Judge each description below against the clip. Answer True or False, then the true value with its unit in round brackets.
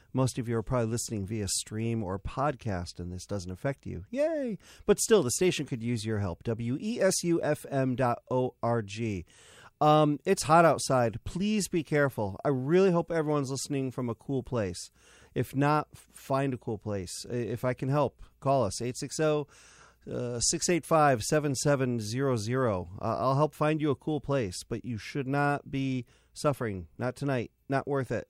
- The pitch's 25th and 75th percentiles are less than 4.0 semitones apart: False (4.5 semitones)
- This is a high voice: False (130 Hz)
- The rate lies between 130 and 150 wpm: False (175 wpm)